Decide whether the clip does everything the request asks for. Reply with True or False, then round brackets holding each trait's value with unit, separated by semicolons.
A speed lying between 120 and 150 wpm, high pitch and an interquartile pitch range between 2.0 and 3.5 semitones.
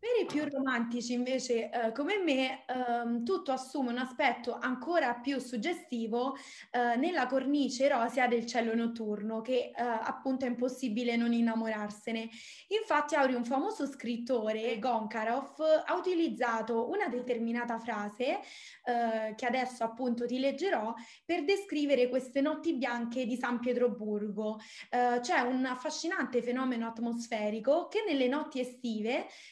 True (135 wpm; 250 Hz; 2.8 semitones)